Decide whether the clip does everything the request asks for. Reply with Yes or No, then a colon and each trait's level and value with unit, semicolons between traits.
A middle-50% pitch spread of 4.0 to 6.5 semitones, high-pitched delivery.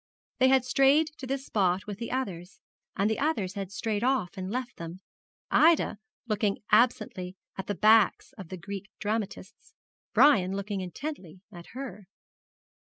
Yes: average, 5.2 semitones; high, 210 Hz